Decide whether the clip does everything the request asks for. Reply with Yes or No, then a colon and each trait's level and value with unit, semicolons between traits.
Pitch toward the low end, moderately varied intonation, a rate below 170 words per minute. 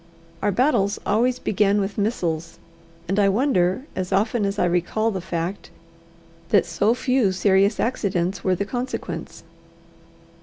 No: high, 200 Hz; average, 3.1 semitones; average, 140 wpm